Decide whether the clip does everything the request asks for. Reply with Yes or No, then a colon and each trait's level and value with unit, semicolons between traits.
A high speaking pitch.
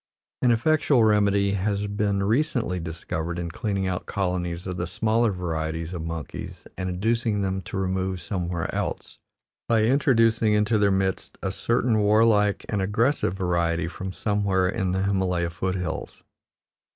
No: very low, 95 Hz